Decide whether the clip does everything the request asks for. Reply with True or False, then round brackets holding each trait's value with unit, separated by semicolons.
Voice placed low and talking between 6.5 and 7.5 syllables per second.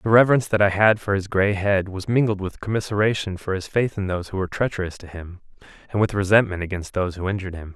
True (100 Hz; 6.8 syllables/s)